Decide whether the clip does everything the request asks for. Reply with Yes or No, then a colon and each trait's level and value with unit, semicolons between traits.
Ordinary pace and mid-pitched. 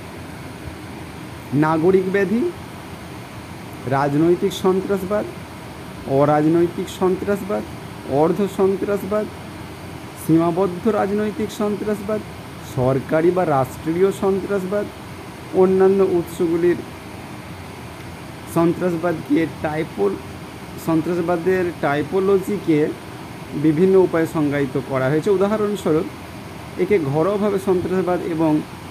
Yes: average, 65 wpm; medium, 180 Hz